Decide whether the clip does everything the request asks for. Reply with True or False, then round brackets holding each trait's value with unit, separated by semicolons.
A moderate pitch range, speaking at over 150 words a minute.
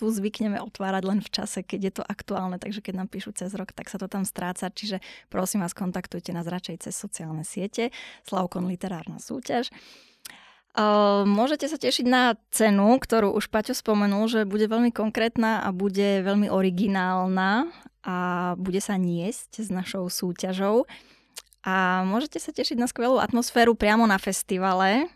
True (3.1 semitones; 160 wpm)